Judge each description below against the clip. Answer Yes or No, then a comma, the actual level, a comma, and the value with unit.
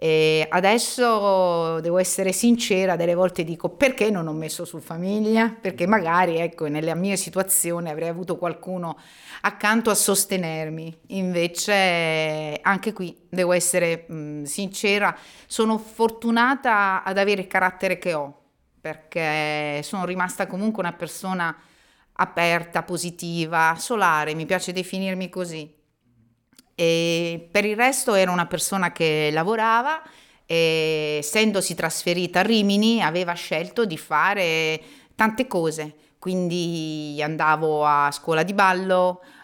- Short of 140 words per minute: Yes, average, 120 wpm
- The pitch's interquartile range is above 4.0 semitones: No, average, 3.4 semitones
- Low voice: No, medium, 175 Hz